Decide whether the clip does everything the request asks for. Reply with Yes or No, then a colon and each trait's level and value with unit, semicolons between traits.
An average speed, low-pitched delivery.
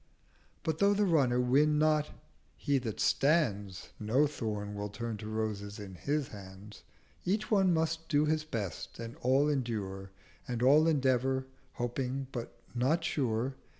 Yes: average, 150 wpm; low, 130 Hz